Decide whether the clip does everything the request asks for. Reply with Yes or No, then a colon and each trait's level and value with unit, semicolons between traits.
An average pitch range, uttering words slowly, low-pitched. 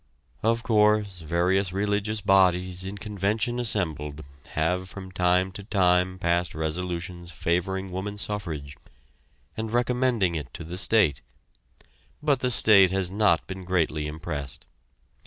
Yes: average, 3.3 semitones; slow, 125 wpm; very low, 95 Hz